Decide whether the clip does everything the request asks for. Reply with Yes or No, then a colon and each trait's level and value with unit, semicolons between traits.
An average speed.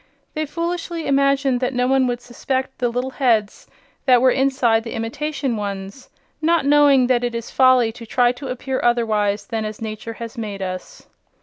Yes: average, 180 wpm